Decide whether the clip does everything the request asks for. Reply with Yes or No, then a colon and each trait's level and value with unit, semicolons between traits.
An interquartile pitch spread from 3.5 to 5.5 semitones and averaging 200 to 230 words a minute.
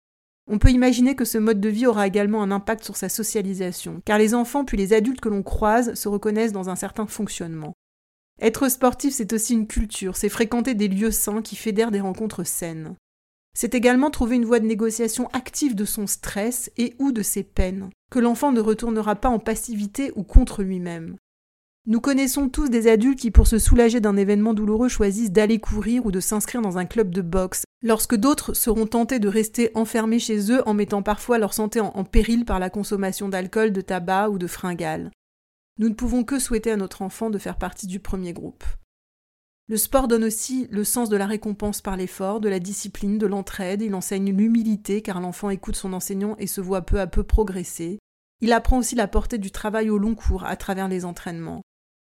No: average, 2.9 semitones; average, 210 wpm